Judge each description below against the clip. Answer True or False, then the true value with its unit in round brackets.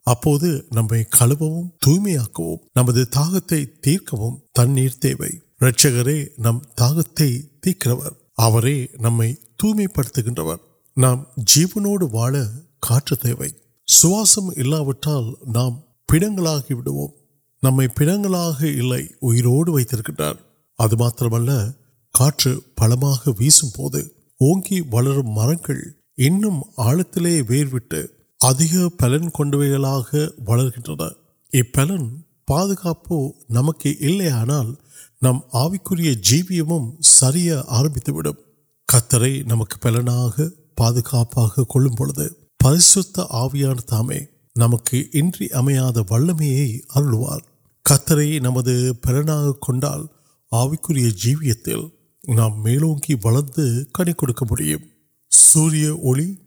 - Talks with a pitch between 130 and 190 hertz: True (135 Hz)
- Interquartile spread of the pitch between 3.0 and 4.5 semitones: True (4.0 semitones)